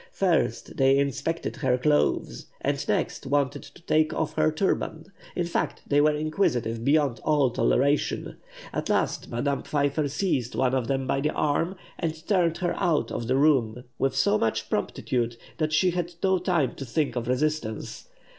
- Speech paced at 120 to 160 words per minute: No, average, 170 wpm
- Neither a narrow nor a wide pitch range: Yes, average, 3.3 semitones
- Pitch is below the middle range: No, medium, 145 Hz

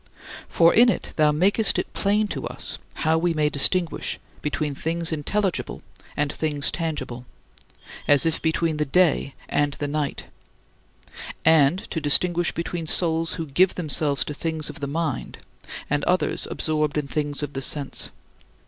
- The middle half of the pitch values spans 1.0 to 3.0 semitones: Yes, narrow, 2.5 semitones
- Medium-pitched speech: Yes, medium, 155 Hz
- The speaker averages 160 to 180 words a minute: No, average, 150 wpm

